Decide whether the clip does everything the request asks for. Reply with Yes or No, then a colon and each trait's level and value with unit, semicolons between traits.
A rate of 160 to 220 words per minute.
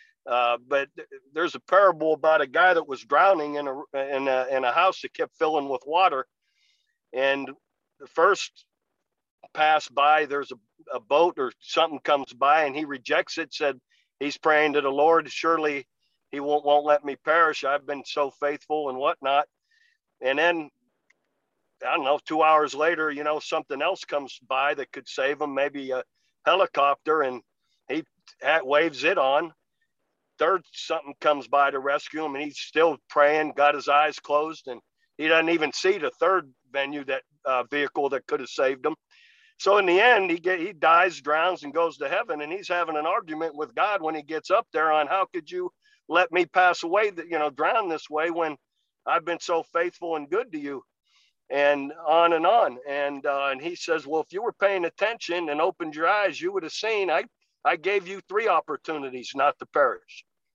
Yes: average, 195 wpm